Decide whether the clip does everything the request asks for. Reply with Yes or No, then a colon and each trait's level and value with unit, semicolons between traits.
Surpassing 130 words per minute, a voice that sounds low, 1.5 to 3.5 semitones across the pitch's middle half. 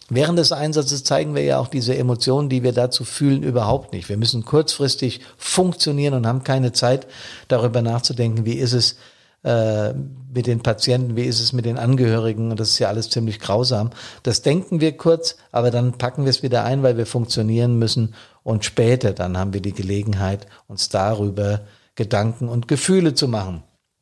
Yes: average, 185 wpm; low, 120 Hz; average, 3.0 semitones